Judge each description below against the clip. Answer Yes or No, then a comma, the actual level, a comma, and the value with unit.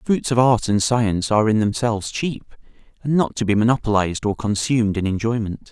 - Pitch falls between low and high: No, low, 110 Hz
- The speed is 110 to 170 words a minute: No, average, 200 wpm